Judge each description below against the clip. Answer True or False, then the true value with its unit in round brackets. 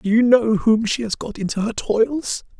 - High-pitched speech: True (225 Hz)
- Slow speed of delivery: False (230 wpm)